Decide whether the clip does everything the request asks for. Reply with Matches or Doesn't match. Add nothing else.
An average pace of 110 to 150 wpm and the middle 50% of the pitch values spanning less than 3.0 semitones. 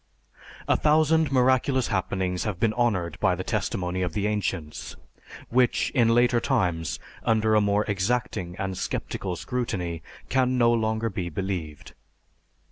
Doesn't match